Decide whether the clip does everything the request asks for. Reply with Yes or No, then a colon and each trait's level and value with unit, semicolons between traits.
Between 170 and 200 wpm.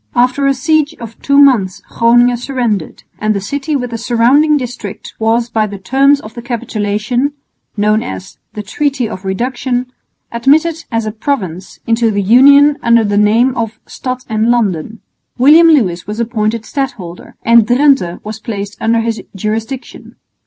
No: average, 160 wpm